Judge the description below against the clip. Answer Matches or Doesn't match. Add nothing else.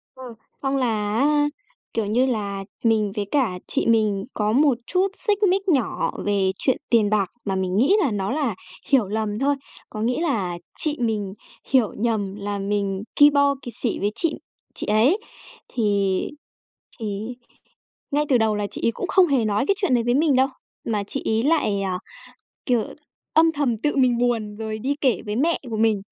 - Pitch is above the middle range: Matches